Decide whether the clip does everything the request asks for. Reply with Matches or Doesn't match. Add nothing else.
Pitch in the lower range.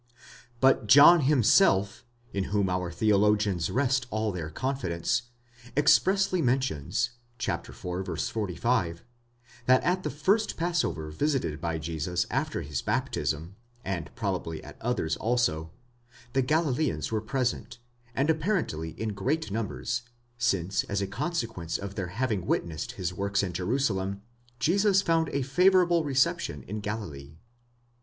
Matches